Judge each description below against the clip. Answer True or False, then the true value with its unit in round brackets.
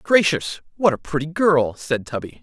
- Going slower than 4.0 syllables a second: False (4.7 syllables/s)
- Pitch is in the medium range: True (155 Hz)